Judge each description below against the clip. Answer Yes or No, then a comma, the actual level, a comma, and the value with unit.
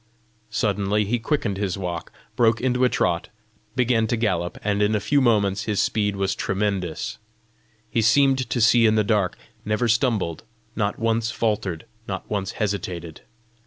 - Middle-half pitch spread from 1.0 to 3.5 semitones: Yes, average, 2.9 semitones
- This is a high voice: No, low, 105 Hz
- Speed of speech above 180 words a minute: No, average, 160 wpm